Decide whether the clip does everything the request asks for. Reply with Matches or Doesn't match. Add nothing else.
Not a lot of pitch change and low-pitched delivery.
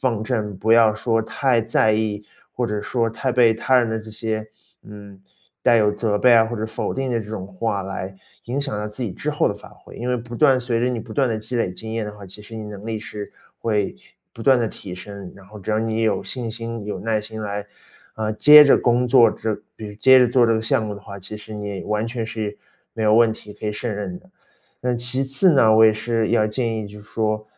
Matches